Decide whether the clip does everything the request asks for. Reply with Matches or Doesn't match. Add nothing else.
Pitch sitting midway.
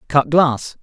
Matches